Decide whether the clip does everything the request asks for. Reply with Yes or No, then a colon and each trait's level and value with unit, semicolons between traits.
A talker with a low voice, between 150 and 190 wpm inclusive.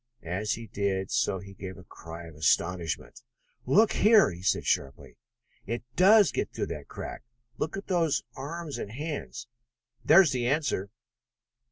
Yes: low, 115 Hz; average, 160 wpm